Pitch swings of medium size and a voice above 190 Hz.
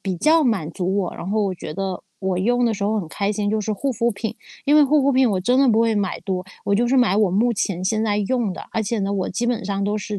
Yes: average, 3.5 semitones; high, 210 Hz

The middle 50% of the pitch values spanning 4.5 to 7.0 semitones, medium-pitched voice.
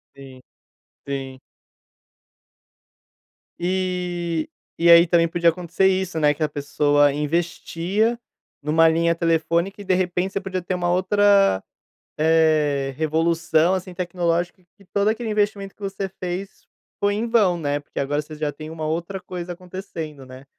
No: average, 3.3 semitones; medium, 170 Hz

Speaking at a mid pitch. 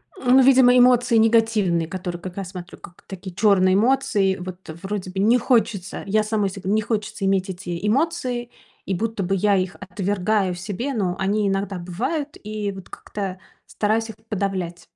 No: high, 200 Hz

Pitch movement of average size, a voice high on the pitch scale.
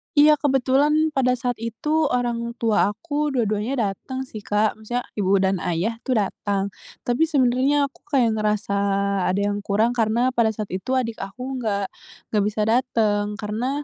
Yes: average, 3.9 semitones; high, 235 Hz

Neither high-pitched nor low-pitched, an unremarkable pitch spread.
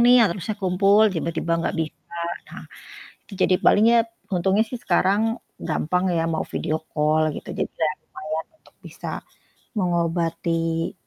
Yes: medium, 175 Hz; average, 3.6 semitones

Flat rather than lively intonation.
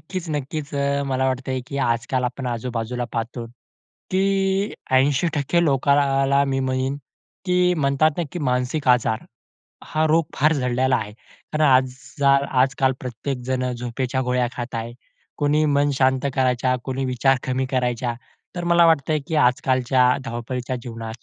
Yes: narrow, 2.1 semitones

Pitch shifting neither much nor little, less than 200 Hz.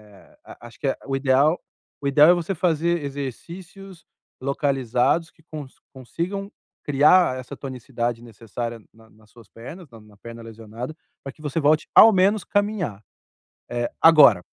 No: wide, 6.0 semitones; medium, 140 Hz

